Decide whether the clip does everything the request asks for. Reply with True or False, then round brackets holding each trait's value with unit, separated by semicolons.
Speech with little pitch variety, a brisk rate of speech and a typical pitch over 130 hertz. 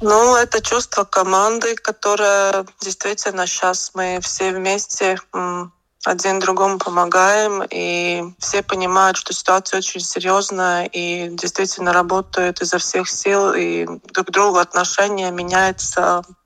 False (1.8 semitones; 115 wpm; 190 Hz)